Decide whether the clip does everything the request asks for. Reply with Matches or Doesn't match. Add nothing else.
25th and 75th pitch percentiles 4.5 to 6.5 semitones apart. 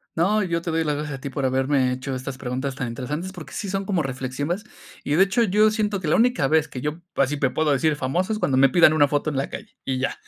Matches